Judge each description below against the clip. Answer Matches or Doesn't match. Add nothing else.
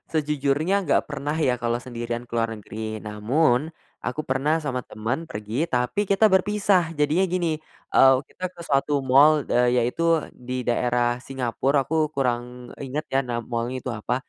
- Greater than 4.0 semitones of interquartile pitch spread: Matches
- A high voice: Doesn't match